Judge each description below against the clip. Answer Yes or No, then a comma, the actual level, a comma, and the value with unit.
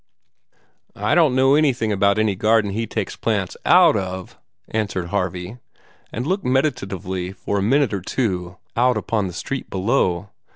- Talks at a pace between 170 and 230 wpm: No, average, 160 wpm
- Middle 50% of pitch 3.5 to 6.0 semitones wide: Yes, average, 5.1 semitones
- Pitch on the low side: Yes, low, 105 Hz